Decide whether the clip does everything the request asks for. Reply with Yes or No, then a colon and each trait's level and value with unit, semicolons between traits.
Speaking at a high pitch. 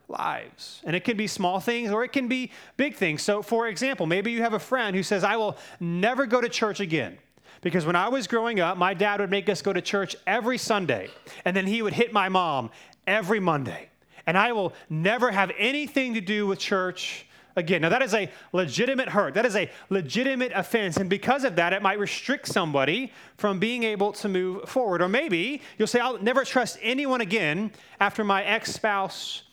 Yes: high, 205 Hz